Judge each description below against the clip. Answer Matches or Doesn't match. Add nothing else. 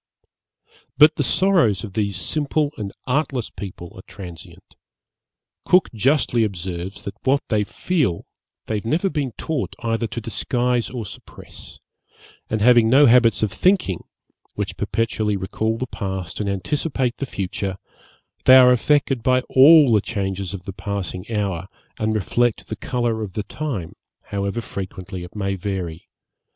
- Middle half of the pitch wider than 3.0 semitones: Matches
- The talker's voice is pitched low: Matches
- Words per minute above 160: Doesn't match